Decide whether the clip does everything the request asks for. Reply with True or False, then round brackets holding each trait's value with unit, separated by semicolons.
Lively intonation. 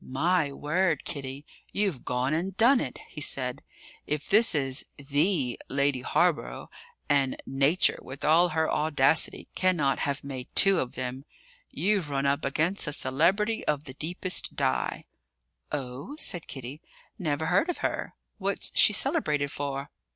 False (4.8 semitones)